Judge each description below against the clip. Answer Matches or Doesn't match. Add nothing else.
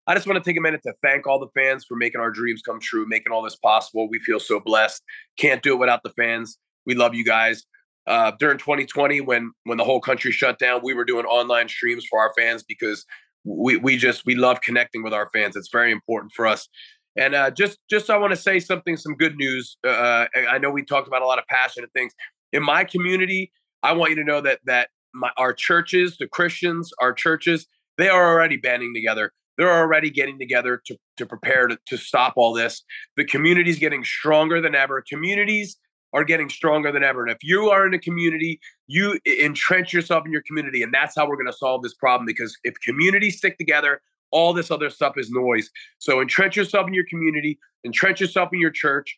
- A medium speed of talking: Doesn't match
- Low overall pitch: Doesn't match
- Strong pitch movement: Matches